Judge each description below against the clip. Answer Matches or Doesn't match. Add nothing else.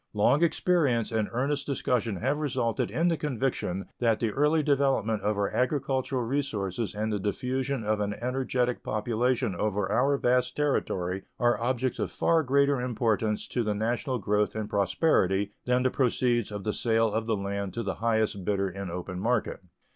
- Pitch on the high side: Doesn't match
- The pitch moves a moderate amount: Matches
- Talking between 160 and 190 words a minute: Matches